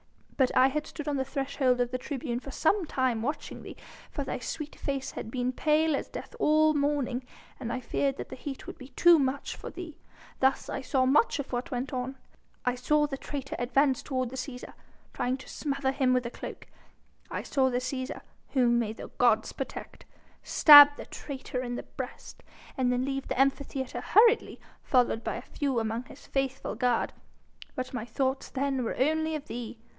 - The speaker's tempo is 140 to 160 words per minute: No, average, 200 wpm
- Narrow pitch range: Yes, narrow, 2.2 semitones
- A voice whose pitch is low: No, very high, 265 Hz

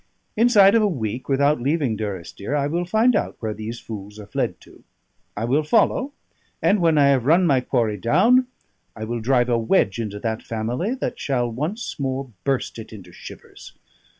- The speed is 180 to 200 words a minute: Yes, average, 185 wpm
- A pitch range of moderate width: No, wide, 7.1 semitones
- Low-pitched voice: Yes, low, 130 Hz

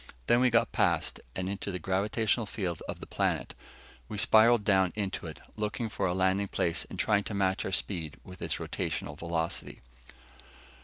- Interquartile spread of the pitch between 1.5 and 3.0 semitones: Yes, narrow, 2.6 semitones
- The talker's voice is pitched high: No, low, 100 Hz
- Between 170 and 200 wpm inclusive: Yes, average, 175 wpm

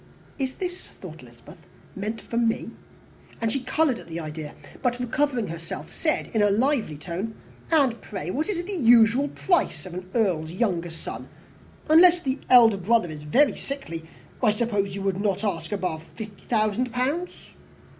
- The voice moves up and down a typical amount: No, wide, 6.3 semitones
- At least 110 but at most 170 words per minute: Yes, average, 165 wpm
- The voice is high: Yes, high, 225 Hz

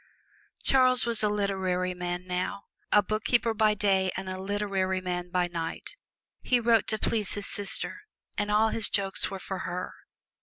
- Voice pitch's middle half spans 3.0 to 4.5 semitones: No, narrow, 2.6 semitones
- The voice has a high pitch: Yes, high, 200 Hz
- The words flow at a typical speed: Yes, average, 165 wpm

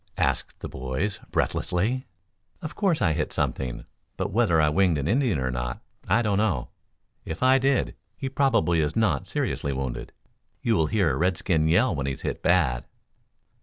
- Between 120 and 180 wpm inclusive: Yes, average, 165 wpm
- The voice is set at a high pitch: No, very low, 90 Hz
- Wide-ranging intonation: Yes, wide, 7.8 semitones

